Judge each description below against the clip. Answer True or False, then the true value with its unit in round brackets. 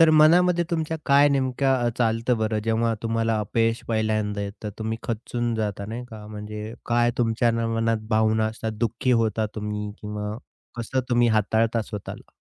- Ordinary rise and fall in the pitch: False (1.8 semitones)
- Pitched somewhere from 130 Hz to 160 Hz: False (115 Hz)